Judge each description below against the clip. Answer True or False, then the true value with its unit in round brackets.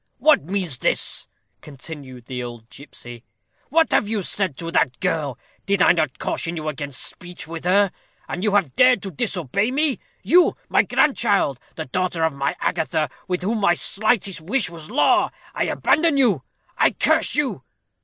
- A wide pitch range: True (6.3 semitones)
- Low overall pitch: False (175 Hz)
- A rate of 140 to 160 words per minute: False (170 wpm)